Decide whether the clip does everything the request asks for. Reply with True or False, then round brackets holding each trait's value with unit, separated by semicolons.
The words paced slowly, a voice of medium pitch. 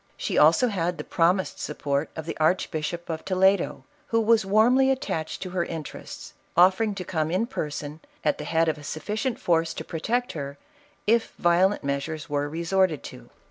False (175 wpm; 170 Hz)